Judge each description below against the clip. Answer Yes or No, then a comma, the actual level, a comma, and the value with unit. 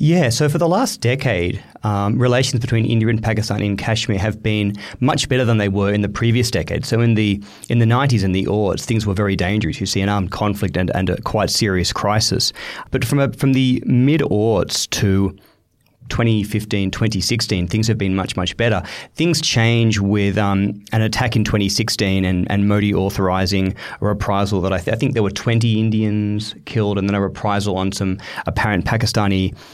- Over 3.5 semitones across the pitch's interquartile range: No, average, 2.8 semitones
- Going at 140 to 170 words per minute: No, average, 195 wpm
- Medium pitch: No, low, 105 Hz